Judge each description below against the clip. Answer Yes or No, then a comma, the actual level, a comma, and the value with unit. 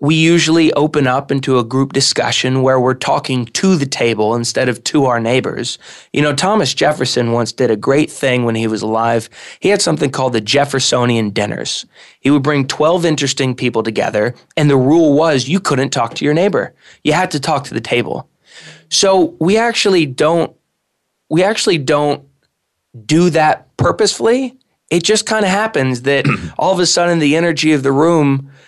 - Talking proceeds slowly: No, average, 185 wpm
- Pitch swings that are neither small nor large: Yes, average, 4.5 semitones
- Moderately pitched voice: Yes, medium, 145 Hz